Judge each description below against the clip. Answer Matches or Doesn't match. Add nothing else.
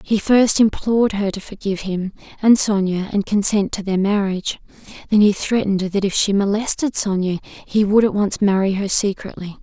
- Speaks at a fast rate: Doesn't match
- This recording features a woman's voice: Matches